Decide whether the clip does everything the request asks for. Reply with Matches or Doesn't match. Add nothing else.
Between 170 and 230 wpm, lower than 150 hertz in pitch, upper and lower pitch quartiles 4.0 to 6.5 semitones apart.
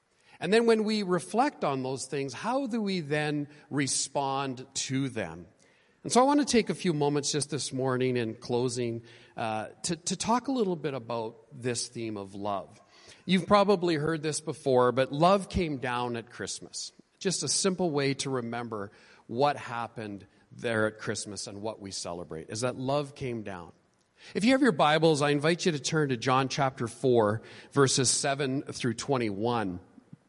Matches